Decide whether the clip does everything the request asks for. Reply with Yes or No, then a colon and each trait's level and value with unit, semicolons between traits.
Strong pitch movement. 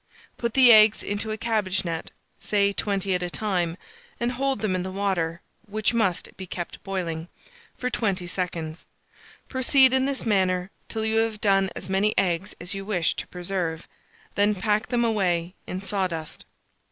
No: average, 3.4 semitones